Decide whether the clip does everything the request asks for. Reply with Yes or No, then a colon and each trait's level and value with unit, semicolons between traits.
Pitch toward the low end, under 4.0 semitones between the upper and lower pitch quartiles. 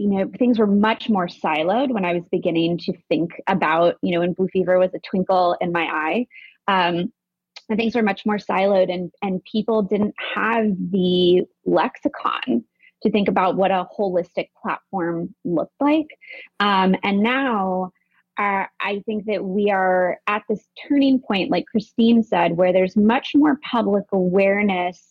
No: high, 195 Hz; average, 3.3 semitones